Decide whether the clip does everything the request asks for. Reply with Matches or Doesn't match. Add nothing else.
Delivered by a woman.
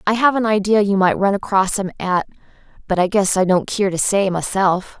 Matches